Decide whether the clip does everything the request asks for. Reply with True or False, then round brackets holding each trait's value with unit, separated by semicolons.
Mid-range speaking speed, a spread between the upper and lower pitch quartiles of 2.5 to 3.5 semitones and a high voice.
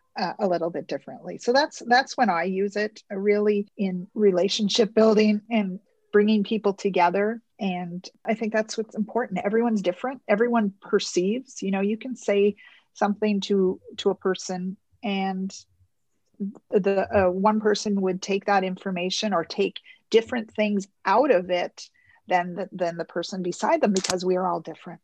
True (165 wpm; 2.9 semitones; 200 Hz)